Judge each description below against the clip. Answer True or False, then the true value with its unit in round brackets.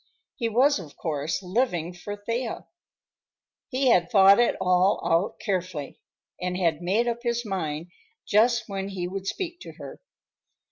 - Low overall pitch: False (195 Hz)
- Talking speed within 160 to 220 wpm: False (150 wpm)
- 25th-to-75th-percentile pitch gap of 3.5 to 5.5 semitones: True (4.9 semitones)